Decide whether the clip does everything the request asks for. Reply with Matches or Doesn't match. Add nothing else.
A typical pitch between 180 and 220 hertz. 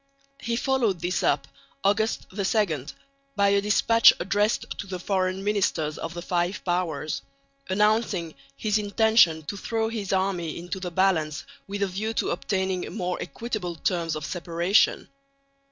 Matches